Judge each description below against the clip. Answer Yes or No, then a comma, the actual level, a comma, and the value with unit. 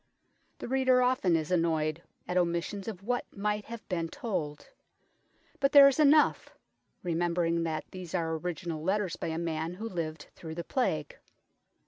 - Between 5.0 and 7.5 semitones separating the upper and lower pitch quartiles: Yes, wide, 5.5 semitones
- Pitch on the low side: No, medium, 180 Hz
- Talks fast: No, average, 155 wpm